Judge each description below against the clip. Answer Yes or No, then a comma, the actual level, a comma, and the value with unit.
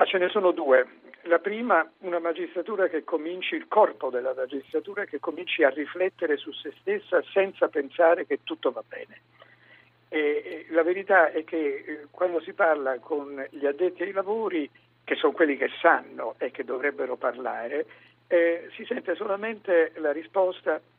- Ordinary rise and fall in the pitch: No, wide, 6.6 semitones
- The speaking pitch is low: No, medium, 180 Hz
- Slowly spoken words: No, average, 165 wpm